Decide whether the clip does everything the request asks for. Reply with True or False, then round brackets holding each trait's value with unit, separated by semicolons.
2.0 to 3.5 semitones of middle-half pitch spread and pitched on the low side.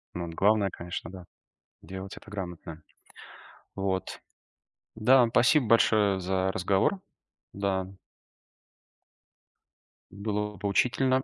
True (2.5 semitones; 100 Hz)